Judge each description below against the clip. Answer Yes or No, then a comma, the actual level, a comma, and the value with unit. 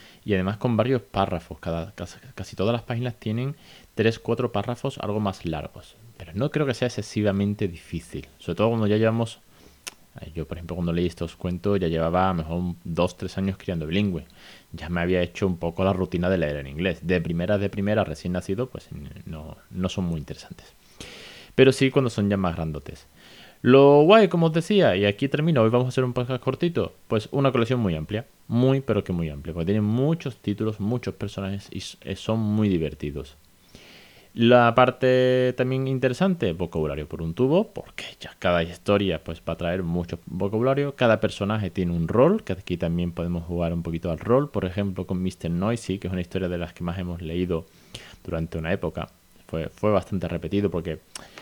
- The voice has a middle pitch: No, very low, 95 Hz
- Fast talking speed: Yes, fast, 195 wpm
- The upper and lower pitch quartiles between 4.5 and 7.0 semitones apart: Yes, average, 5.2 semitones